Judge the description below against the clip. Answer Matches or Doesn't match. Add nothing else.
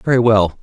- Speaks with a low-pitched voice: Matches